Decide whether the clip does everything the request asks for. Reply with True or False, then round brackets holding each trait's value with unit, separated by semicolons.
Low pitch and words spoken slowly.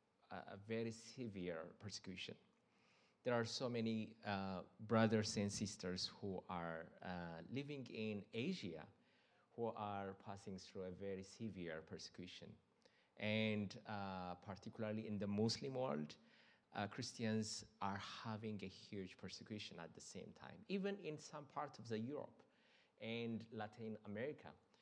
True (105 Hz; 130 wpm)